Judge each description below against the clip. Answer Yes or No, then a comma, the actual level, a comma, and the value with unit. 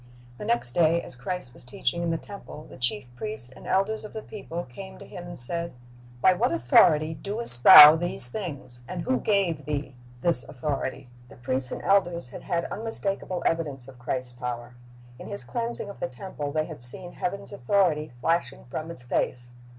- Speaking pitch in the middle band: Yes, medium, 160 Hz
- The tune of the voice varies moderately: No, wide, 6.7 semitones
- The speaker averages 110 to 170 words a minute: No, average, 190 wpm